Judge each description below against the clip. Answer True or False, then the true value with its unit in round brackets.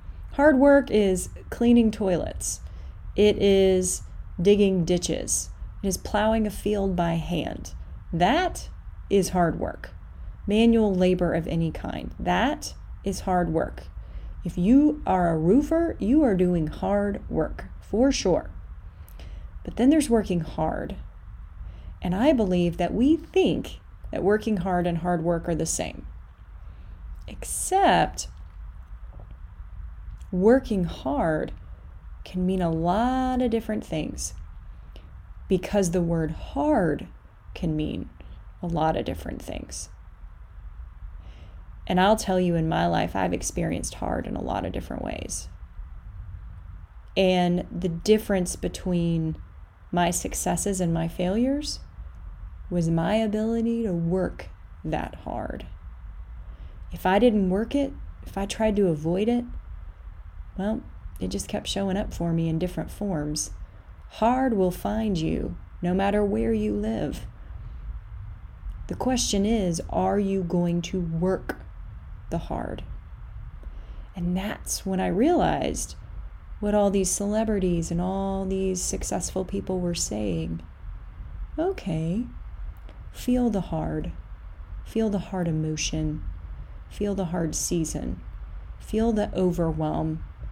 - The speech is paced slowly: True (125 wpm)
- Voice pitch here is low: False (170 Hz)